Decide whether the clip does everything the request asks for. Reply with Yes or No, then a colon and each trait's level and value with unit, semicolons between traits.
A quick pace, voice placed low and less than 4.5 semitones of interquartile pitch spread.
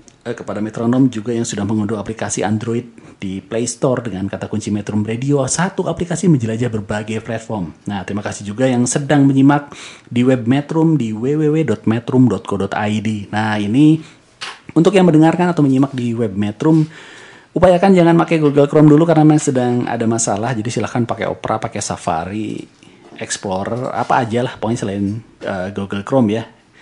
No: fast, 155 wpm; low, 115 Hz; average, 5.2 semitones